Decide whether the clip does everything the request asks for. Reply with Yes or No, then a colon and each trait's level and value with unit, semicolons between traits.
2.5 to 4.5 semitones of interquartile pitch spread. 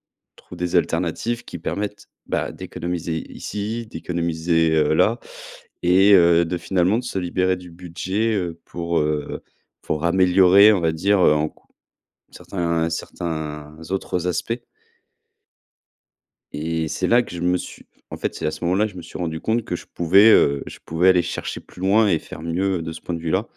Yes: average, 2.8 semitones